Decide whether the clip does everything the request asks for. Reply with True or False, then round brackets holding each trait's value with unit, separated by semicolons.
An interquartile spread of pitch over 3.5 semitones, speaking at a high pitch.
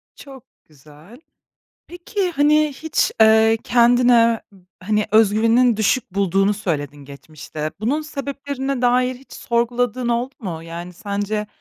True (4.6 semitones; 230 Hz)